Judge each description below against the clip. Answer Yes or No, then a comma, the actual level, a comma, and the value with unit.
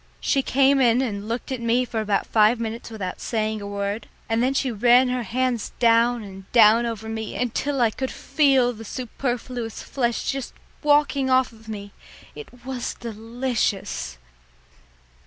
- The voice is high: Yes, high, 235 Hz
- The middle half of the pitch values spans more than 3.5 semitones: No, average, 2.7 semitones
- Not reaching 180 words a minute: Yes, average, 160 wpm